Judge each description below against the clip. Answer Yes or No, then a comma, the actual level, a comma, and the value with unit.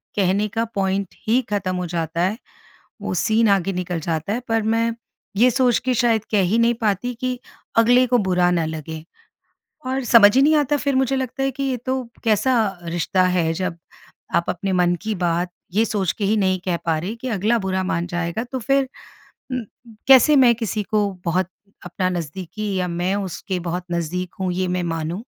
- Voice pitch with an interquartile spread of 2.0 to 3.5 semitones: No, average, 4.8 semitones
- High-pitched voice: Yes, high, 195 Hz